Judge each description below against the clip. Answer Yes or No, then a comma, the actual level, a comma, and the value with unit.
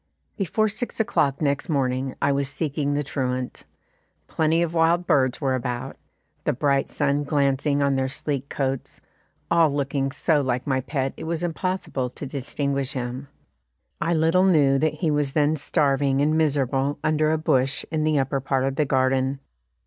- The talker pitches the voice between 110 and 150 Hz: Yes, medium, 140 Hz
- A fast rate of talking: No, average, 170 wpm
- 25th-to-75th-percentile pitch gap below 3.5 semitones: Yes, narrow, 2.6 semitones